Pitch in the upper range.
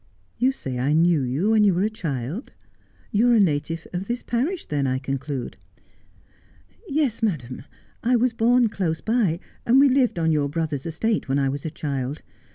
No: medium, 170 Hz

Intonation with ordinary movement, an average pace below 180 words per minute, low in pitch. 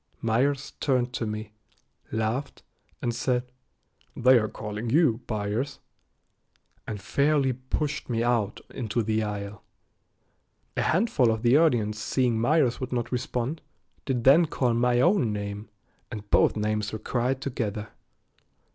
Yes: average, 3.4 semitones; slow, 135 wpm; low, 120 Hz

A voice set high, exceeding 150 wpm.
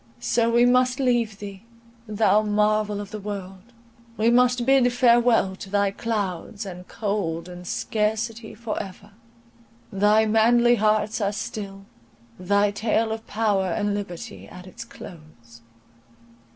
No: high, 210 Hz; slow, 135 wpm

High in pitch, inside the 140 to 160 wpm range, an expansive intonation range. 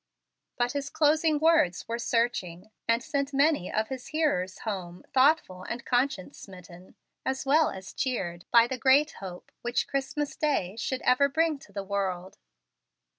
Yes: high, 245 Hz; average, 155 wpm; wide, 6.9 semitones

